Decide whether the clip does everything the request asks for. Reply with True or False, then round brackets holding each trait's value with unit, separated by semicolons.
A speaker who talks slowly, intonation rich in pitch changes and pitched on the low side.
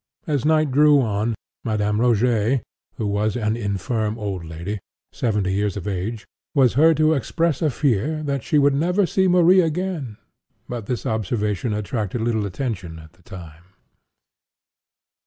False (150 wpm; 5.9 semitones; 115 Hz)